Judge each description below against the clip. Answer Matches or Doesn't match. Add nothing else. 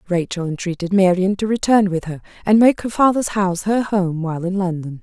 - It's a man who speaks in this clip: Doesn't match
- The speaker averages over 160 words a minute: Matches